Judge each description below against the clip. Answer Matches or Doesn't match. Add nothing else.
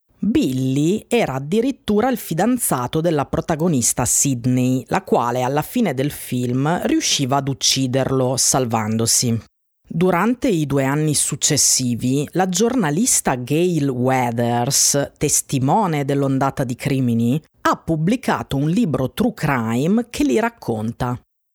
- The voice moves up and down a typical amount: Doesn't match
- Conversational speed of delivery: Doesn't match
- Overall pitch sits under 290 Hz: Matches